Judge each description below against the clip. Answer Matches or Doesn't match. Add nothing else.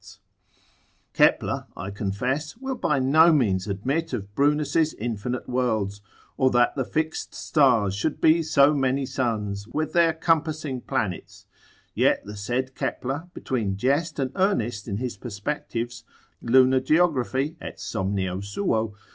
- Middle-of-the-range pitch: Doesn't match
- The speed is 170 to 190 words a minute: Doesn't match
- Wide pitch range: Matches